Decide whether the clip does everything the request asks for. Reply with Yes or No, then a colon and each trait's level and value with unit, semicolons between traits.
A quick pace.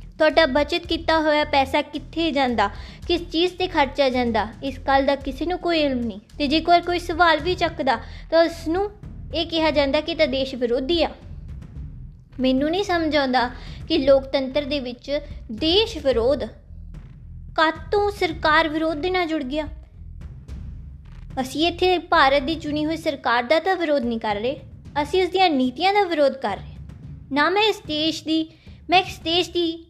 Yes: fast, 170 wpm